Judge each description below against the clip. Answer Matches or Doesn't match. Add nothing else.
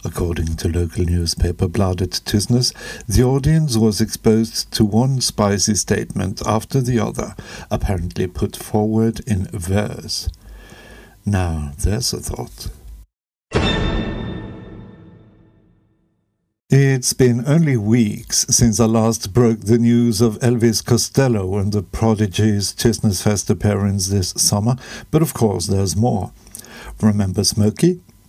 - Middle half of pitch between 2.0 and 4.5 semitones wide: Matches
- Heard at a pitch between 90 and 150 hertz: Matches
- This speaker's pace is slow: Matches